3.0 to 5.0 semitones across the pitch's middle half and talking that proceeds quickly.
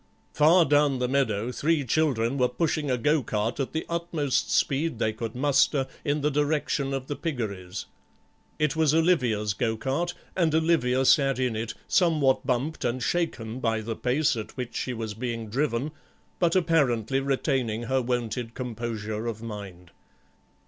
No: average, 4.5 semitones; average, 160 wpm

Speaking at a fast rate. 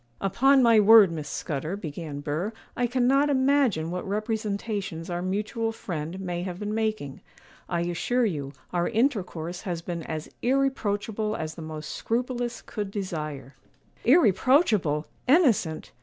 No: slow, 135 wpm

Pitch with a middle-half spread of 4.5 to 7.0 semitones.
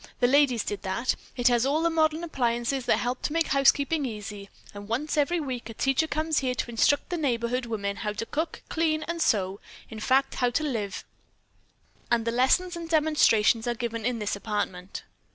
Yes: wide, 5.4 semitones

